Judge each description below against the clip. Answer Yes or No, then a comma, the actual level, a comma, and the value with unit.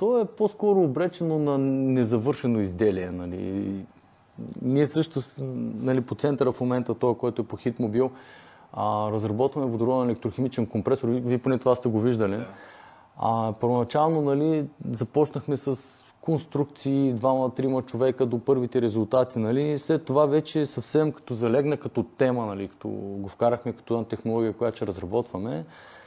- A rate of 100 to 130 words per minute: No, average, 145 wpm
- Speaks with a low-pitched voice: Yes, low, 125 Hz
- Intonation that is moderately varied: Yes, average, 3.4 semitones